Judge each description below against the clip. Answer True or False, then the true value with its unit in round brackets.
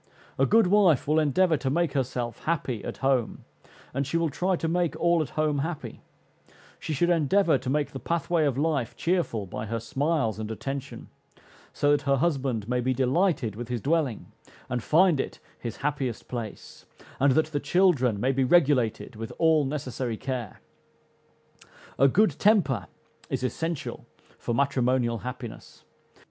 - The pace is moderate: True (160 wpm)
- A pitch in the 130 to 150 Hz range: True (140 Hz)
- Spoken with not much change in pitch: False (4.6 semitones)